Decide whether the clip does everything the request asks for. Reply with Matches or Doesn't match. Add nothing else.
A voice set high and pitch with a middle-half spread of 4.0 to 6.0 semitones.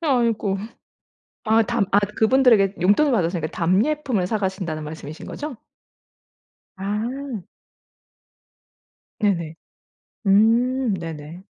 Matches